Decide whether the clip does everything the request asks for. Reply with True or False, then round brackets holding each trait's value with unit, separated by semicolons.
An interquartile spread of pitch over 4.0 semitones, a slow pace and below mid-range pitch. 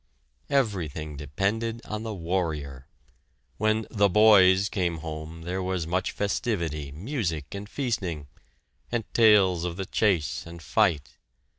True (4.9 semitones; 125 wpm; 95 Hz)